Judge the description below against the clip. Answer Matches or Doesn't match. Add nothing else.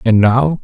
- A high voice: Doesn't match